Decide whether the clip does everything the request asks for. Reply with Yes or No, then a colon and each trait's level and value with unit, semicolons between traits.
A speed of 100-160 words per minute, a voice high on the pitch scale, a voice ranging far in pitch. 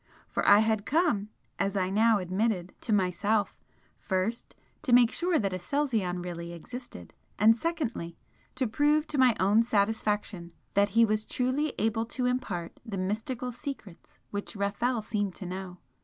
No: average, 155 wpm; high, 215 Hz; average, 4.4 semitones